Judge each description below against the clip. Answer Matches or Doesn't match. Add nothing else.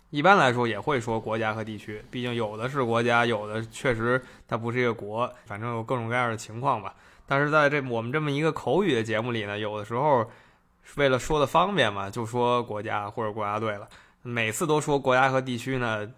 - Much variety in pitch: Doesn't match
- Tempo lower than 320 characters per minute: Doesn't match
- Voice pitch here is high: Doesn't match